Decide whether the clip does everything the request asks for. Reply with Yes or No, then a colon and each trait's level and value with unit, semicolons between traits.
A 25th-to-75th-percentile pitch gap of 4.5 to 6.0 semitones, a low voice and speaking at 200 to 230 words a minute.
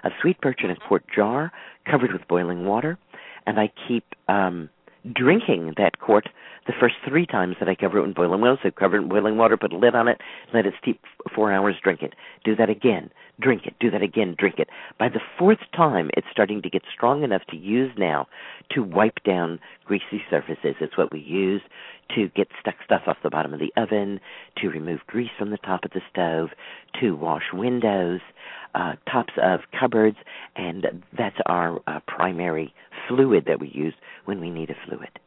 No: average, 4.0 semitones; low, 100 Hz; fast, 205 wpm